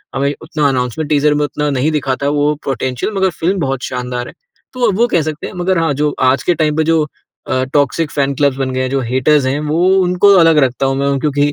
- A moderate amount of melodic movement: Yes, average, 3.1 semitones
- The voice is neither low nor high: Yes, medium, 145 Hz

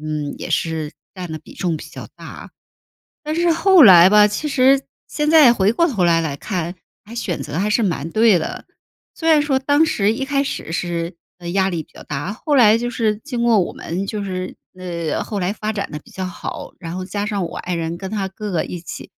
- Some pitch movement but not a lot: No, wide, 5.7 semitones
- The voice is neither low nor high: No, high, 195 Hz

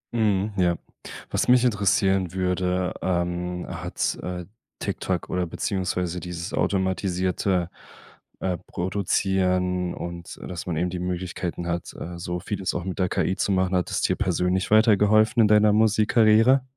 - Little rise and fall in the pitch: Yes, narrow, 2.2 semitones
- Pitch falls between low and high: No, very low, 90 Hz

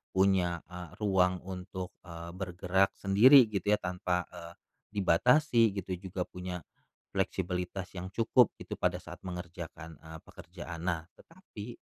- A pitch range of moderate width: No, narrow, 1.9 semitones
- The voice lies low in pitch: Yes, very low, 90 Hz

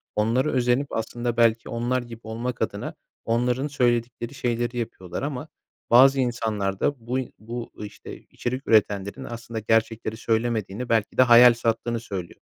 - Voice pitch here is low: Yes, low, 120 Hz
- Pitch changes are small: Yes, narrow, 1.7 semitones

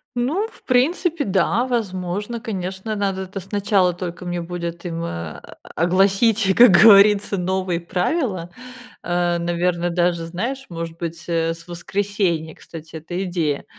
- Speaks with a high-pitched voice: No, medium, 180 Hz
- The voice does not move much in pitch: No, average, 3.2 semitones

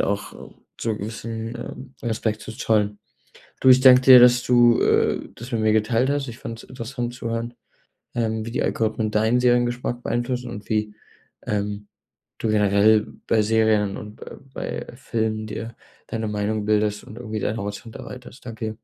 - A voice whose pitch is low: Yes, low, 110 Hz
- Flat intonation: Yes, narrow, 2.2 semitones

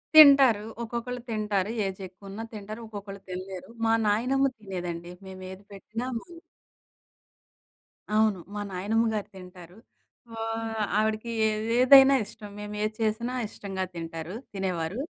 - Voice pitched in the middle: No, high, 210 Hz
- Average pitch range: Yes, average, 3.1 semitones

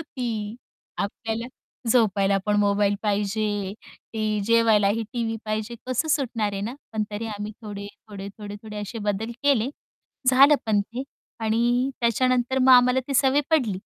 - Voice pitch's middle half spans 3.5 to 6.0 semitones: No, average, 3.1 semitones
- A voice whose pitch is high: Yes, high, 220 Hz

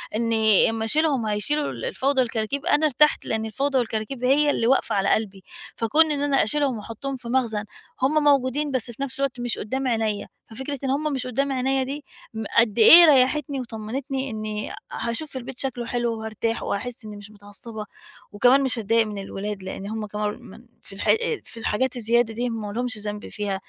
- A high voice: Yes, high, 240 Hz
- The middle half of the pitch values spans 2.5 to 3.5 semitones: No, average, 4.0 semitones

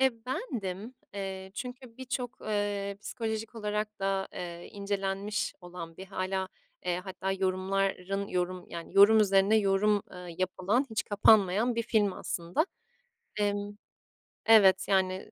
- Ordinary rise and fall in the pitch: No, narrow, 2.2 semitones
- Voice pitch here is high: Yes, high, 200 Hz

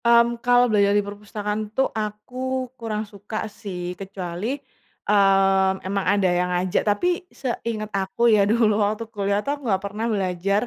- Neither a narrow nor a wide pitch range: No, narrow, 2.1 semitones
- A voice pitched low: No, high, 205 Hz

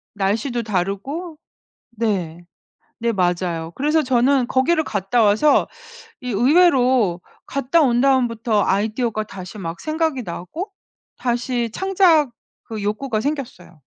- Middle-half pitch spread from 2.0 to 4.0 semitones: No, wide, 5.5 semitones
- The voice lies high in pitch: Yes, high, 235 Hz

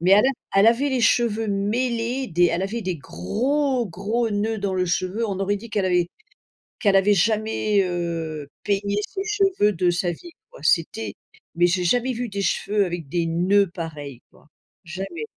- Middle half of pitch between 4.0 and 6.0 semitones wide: Yes, average, 4.6 semitones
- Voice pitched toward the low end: No, high, 200 Hz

